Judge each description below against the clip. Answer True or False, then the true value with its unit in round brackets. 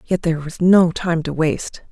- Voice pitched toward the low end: False (170 Hz)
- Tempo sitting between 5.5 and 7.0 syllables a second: False (5.1 syllables/s)